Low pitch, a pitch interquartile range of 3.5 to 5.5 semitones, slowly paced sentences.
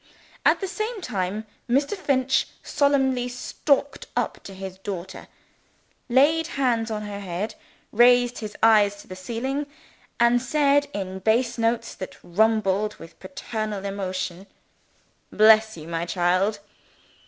No: high, 220 Hz; average, 4.9 semitones; slow, 130 wpm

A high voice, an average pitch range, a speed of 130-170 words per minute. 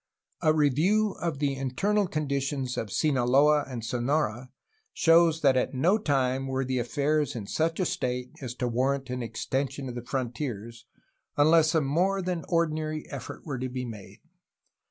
No: medium, 140 Hz; average, 3.7 semitones; average, 160 wpm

